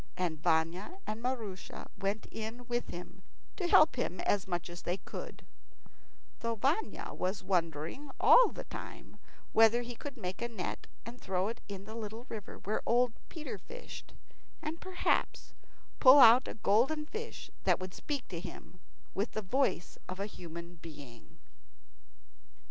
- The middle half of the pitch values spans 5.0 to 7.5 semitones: Yes, wide, 5.5 semitones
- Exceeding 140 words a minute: Yes, average, 155 wpm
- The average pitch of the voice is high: Yes, high, 215 Hz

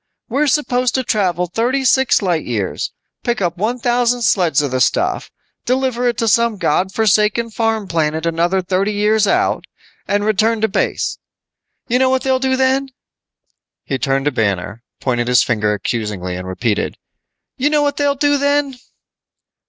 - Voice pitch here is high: Yes, high, 215 Hz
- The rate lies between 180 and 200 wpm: No, average, 165 wpm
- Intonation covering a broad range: Yes, wide, 8.3 semitones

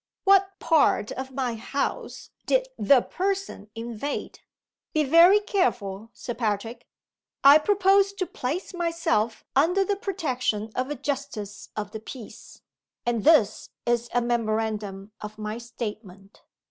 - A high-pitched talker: Yes, very high, 250 Hz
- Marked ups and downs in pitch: Yes, wide, 7.5 semitones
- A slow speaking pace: Yes, slow, 130 wpm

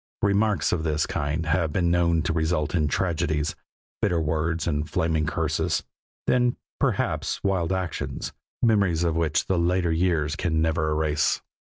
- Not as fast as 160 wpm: Yes, average, 150 wpm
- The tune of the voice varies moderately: No, narrow, 2.3 semitones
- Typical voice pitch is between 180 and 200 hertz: No, very low, 80 Hz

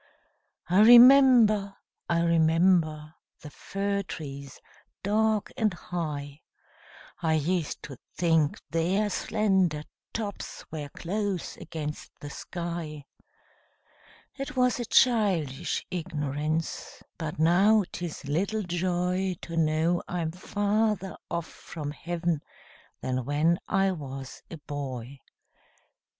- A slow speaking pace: Yes, slow, 105 wpm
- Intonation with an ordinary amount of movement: Yes, average, 4.5 semitones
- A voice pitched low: No, medium, 170 Hz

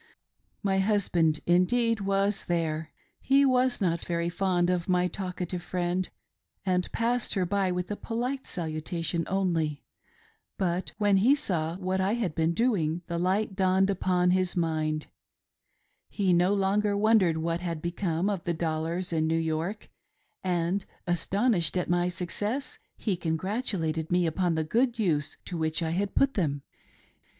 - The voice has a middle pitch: Yes, medium, 180 Hz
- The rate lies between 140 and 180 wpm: Yes, average, 155 wpm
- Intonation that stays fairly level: No, average, 3.1 semitones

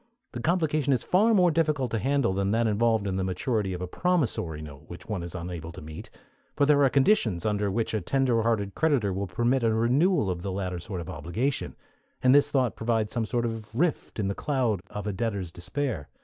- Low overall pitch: Yes, low, 110 Hz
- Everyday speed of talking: No, fast, 220 wpm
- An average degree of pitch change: No, wide, 6.1 semitones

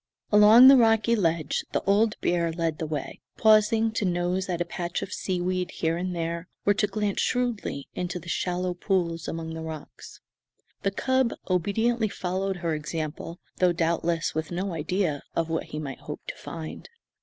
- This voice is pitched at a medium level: Yes, medium, 180 Hz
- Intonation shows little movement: No, average, 3.7 semitones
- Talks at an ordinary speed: Yes, average, 175 wpm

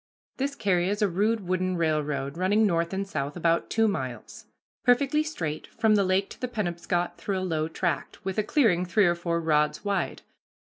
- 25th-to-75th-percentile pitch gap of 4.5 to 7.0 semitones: No, average, 3.7 semitones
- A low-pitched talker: No, medium, 185 Hz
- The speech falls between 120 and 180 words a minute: No, average, 190 wpm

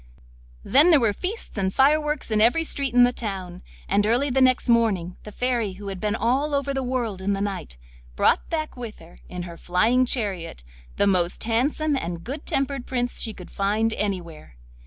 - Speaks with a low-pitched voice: No, high, 225 Hz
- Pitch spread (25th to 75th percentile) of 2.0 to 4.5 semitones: No, wide, 5.4 semitones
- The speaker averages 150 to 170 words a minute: No, average, 195 wpm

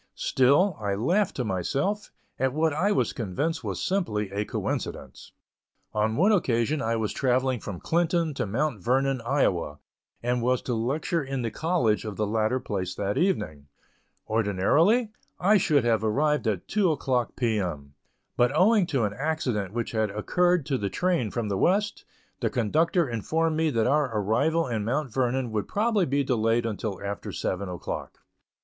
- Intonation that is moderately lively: No, wide, 6.8 semitones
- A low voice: Yes, low, 125 Hz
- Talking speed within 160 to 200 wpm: Yes, average, 170 wpm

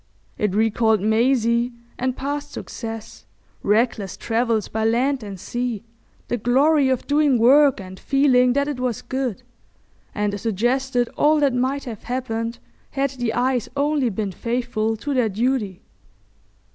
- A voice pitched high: Yes, high, 245 Hz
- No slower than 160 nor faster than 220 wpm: No, average, 140 wpm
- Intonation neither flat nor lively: Yes, average, 3.2 semitones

